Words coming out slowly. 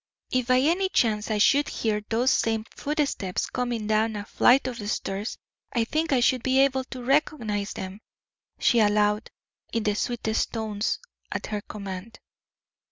No: average, 160 wpm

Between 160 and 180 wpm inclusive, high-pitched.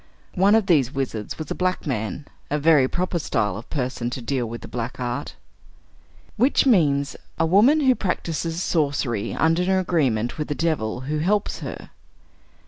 No: average, 170 wpm; medium, 150 Hz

